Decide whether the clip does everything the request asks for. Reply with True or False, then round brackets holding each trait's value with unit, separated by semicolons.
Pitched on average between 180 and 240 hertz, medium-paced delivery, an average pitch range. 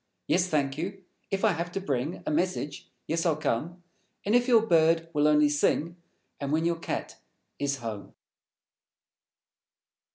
False (165 Hz; 155 wpm; 3.5 semitones)